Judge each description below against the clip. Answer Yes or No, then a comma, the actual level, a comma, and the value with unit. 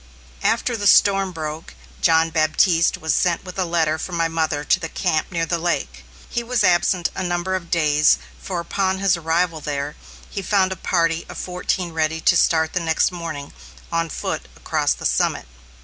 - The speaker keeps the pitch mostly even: Yes, narrow, 2.3 semitones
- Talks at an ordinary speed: Yes, average, 180 wpm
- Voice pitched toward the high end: No, medium, 170 Hz